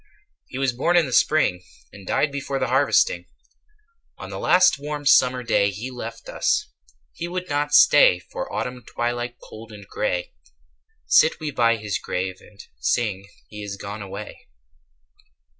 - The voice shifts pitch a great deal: Yes, wide, 6.0 semitones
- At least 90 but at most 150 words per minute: No, average, 160 wpm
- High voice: No, low, 120 Hz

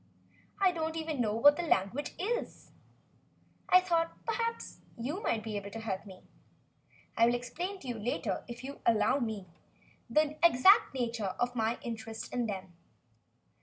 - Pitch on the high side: Yes, high, 245 Hz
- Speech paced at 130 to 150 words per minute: No, average, 165 wpm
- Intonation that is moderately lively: No, wide, 6.5 semitones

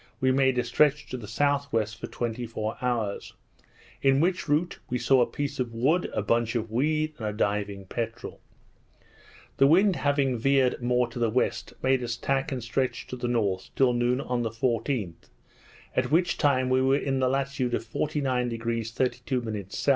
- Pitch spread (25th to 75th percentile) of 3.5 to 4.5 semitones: No, average, 3.0 semitones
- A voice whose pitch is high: No, low, 125 Hz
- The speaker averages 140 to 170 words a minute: No, average, 185 wpm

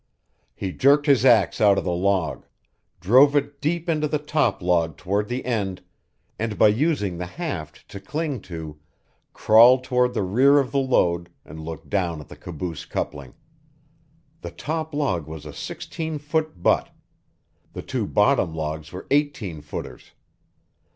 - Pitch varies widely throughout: Yes, wide, 8.8 semitones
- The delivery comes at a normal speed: Yes, average, 155 wpm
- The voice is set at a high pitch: No, low, 105 Hz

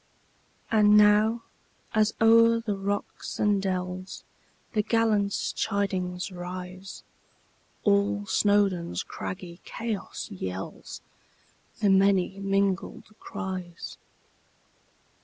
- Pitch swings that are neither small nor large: No, narrow, 2.2 semitones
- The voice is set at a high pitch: Yes, high, 200 Hz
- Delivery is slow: Yes, slow, 70 wpm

